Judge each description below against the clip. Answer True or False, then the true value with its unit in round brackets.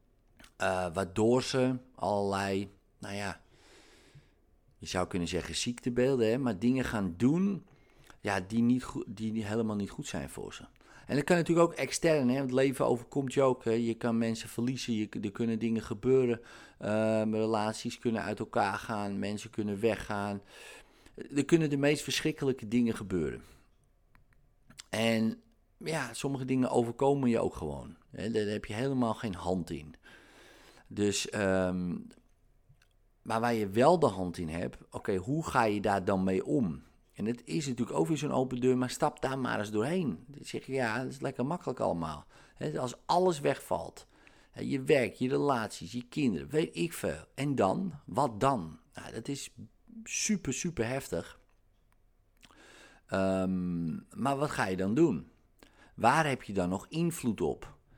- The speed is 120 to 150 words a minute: False (170 wpm)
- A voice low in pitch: True (115 Hz)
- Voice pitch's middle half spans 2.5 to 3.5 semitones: False (4.9 semitones)